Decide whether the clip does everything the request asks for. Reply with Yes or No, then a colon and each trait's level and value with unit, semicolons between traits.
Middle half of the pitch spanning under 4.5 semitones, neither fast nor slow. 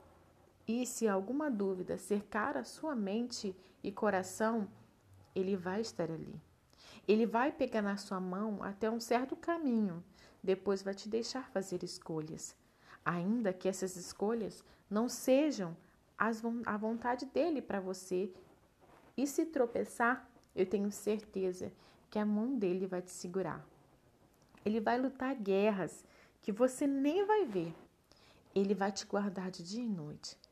Yes: average, 4.0 semitones; average, 140 wpm